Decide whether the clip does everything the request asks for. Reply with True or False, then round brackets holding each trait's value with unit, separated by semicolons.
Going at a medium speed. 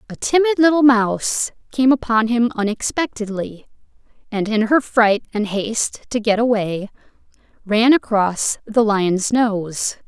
False (130 wpm)